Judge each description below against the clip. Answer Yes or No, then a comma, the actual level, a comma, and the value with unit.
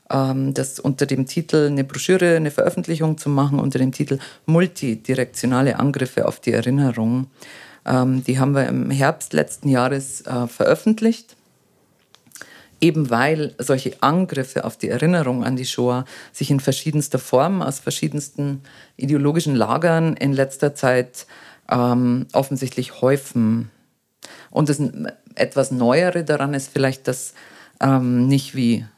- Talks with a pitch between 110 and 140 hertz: Yes, low, 135 Hz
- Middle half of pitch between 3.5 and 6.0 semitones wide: No, narrow, 2.6 semitones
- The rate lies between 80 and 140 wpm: Yes, average, 130 wpm